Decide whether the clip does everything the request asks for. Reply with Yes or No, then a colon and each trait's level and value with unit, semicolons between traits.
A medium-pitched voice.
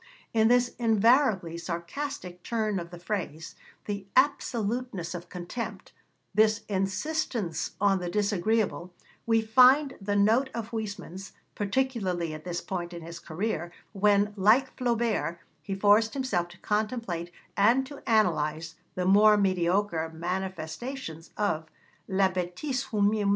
No: high, 200 Hz